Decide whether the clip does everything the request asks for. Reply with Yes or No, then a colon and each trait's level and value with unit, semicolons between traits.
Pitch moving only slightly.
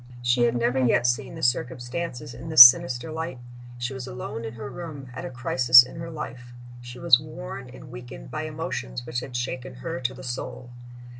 Yes: narrow, 1.4 semitones